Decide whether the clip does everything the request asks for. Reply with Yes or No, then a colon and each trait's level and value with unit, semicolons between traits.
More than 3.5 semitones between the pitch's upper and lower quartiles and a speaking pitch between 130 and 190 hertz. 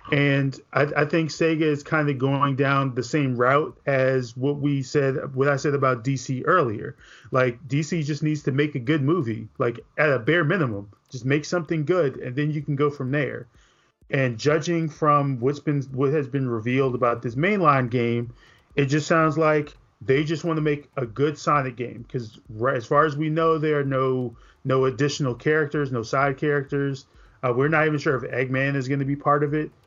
No: narrow, 2.6 semitones; medium, 140 Hz